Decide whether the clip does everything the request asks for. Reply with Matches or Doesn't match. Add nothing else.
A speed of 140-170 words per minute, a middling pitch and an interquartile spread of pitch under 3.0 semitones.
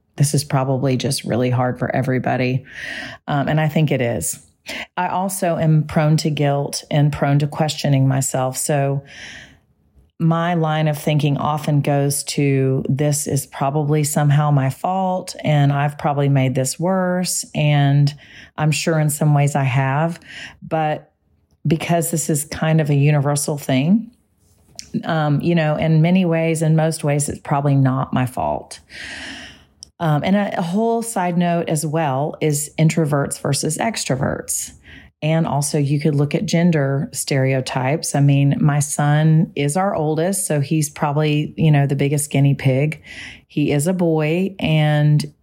Matches